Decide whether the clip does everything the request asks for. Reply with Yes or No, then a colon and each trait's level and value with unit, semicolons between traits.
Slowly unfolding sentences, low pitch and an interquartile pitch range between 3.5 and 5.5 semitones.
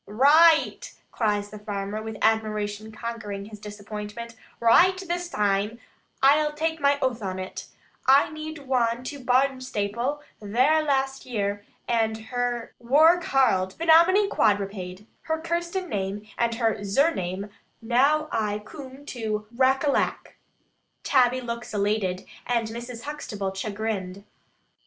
No: slow, 120 wpm; high, 235 Hz; average, 5.2 semitones